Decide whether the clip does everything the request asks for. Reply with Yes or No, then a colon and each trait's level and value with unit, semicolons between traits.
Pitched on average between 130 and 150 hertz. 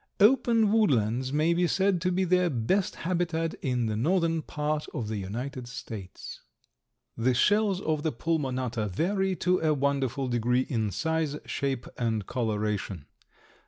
Yes: medium, 140 Hz